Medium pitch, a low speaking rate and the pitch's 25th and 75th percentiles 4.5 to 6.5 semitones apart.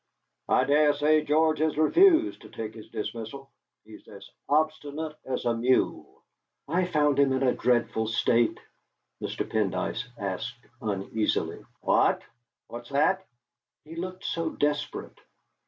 Yes: medium, 145 Hz; slow, 130 wpm; average, 5.0 semitones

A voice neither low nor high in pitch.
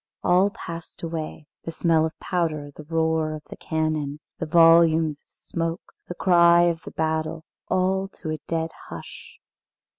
Yes: medium, 165 Hz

